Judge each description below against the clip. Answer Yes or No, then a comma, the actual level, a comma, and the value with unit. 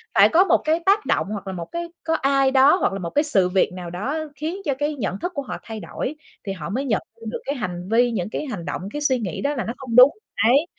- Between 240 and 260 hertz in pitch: Yes, very high, 255 Hz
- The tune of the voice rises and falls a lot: Yes, wide, 7.1 semitones